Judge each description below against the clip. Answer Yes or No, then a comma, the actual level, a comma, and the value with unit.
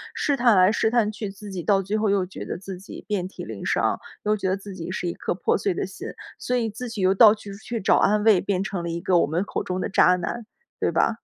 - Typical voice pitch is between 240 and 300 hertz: No, high, 200 Hz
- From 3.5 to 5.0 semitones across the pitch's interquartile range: No, narrow, 2.5 semitones